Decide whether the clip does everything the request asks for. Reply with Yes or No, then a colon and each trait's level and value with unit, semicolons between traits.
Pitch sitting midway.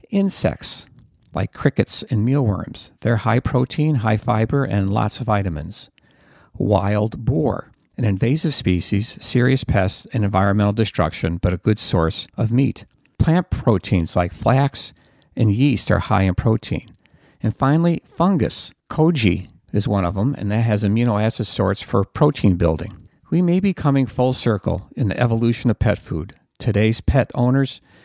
No: low, 110 Hz